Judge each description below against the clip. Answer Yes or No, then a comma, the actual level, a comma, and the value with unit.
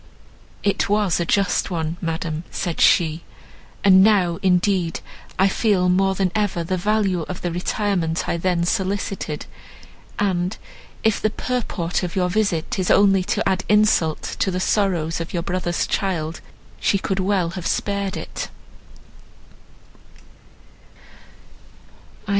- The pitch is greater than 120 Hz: Yes, medium, 185 Hz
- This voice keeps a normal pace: No, slow, 130 wpm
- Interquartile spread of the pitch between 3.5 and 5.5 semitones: No, average, 2.7 semitones